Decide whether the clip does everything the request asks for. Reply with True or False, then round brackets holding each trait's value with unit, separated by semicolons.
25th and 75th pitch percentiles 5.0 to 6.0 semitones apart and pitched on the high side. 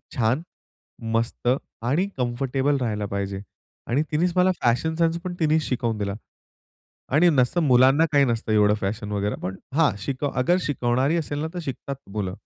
False (5.6 semitones; 130 Hz)